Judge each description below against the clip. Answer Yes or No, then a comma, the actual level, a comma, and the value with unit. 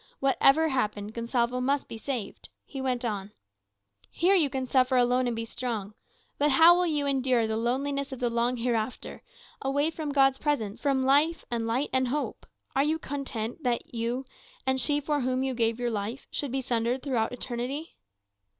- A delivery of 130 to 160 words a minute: No, average, 180 wpm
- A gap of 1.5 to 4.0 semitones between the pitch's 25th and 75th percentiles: Yes, average, 3.0 semitones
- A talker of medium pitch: No, very high, 255 Hz